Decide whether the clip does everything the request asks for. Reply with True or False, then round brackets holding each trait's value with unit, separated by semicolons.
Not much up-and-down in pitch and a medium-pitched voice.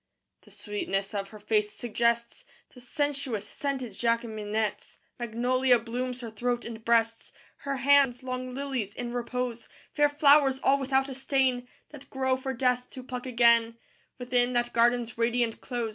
False (2.2 semitones; 245 Hz)